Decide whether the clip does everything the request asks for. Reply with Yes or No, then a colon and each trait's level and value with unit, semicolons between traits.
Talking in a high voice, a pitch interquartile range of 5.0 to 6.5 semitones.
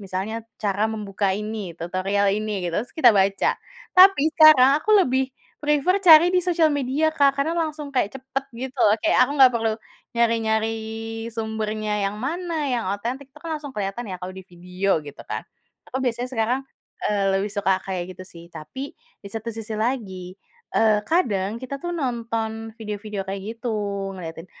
Yes: high, 225 Hz; wide, 5.4 semitones